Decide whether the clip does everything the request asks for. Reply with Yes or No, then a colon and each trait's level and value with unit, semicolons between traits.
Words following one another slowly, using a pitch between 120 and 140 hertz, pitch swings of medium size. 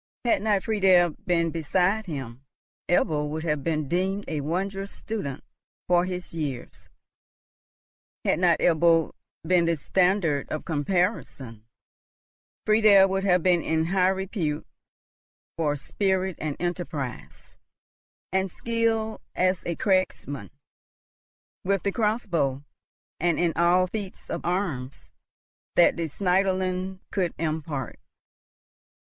No: slow, 115 wpm; medium, 175 Hz; average, 3.4 semitones